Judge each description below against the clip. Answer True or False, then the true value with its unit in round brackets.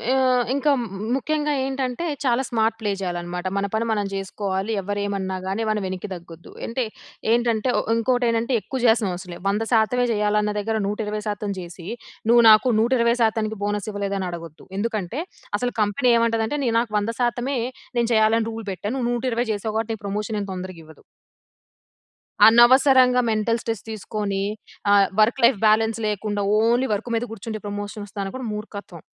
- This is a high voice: True (220 Hz)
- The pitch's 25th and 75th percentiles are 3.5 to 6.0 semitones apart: False (2.9 semitones)